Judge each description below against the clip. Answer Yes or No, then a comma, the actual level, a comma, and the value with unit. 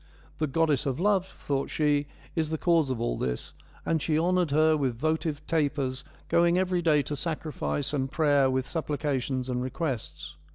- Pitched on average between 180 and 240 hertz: No, medium, 150 Hz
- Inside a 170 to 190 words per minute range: Yes, average, 180 wpm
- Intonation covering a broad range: No, average, 3.3 semitones